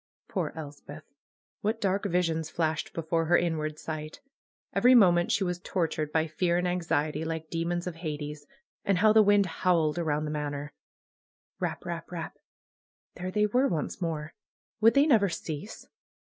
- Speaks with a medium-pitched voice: Yes, medium, 165 Hz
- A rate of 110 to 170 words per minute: Yes, average, 160 wpm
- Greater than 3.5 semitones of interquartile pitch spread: No, average, 3.1 semitones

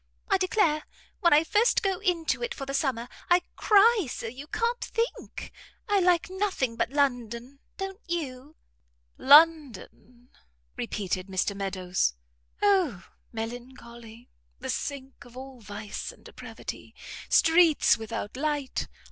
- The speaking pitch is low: No, very high, 275 Hz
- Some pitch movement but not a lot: No, wide, 7.3 semitones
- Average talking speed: No, slow, 125 wpm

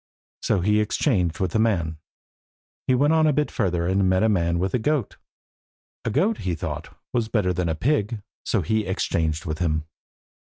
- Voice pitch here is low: Yes, low, 100 Hz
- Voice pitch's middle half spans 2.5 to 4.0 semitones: No, average, 5.1 semitones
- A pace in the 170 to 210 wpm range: Yes, average, 190 wpm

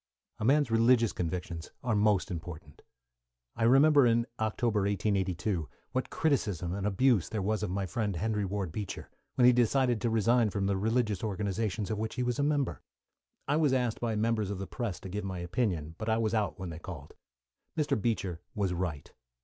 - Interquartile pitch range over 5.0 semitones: No, average, 3.9 semitones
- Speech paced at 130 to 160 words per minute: No, average, 190 wpm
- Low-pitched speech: Yes, low, 105 Hz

